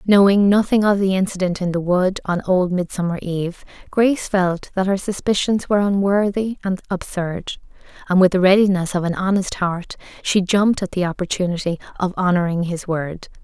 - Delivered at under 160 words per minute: No, average, 170 wpm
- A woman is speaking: Yes, female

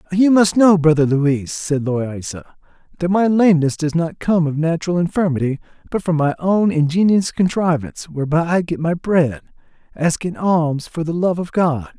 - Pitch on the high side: No, medium, 165 Hz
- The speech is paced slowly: No, average, 170 wpm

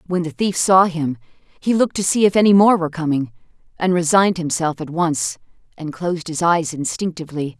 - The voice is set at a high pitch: No, medium, 170 Hz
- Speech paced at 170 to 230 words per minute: Yes, average, 190 wpm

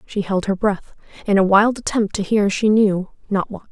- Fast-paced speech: Yes, fast, 225 wpm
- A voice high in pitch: Yes, high, 205 Hz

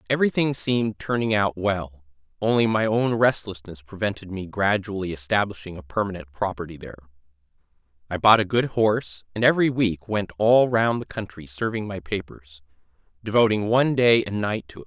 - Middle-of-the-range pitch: No, low, 100 Hz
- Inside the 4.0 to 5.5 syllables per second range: No, 3.6 syllables/s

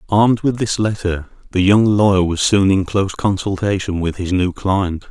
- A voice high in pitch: No, very low, 95 Hz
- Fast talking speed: No, average, 190 wpm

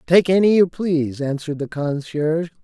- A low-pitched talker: No, medium, 160 Hz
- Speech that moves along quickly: No, average, 160 wpm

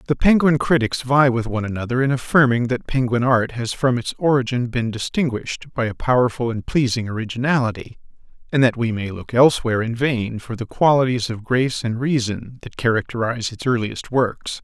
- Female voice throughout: No, male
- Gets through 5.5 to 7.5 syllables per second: Yes, 5.6 syllables/s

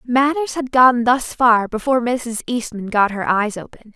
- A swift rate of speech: No, average, 180 wpm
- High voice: Yes, high, 240 Hz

